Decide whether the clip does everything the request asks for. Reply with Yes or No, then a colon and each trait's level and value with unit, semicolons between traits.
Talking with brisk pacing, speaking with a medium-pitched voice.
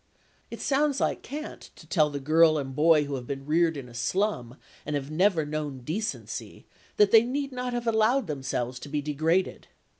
No: average, 190 wpm; medium, 155 Hz